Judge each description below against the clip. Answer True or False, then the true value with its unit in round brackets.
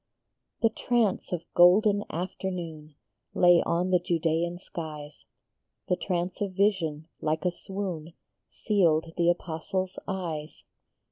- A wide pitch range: False (2.7 semitones)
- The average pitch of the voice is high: False (175 Hz)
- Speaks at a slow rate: True (120 wpm)